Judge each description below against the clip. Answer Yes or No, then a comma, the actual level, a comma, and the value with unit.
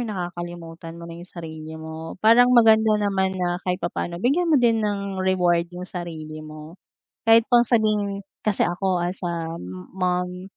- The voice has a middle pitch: Yes, medium, 180 Hz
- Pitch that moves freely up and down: No, average, 3.7 semitones